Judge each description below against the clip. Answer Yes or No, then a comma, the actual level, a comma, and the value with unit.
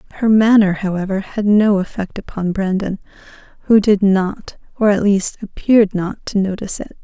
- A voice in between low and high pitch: No, high, 200 Hz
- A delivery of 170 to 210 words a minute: No, average, 160 wpm